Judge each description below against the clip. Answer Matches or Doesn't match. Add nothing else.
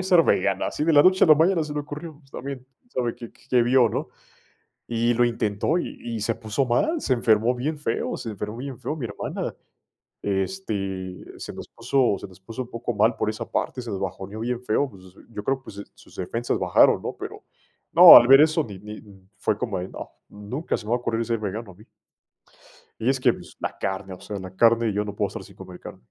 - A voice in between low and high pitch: Doesn't match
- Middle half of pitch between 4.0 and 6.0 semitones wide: Matches